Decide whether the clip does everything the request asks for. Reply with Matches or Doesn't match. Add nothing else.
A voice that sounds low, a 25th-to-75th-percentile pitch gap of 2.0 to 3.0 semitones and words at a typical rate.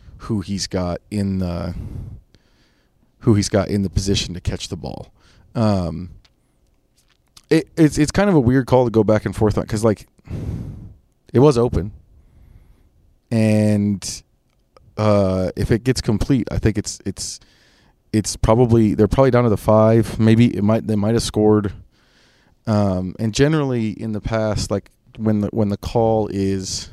Matches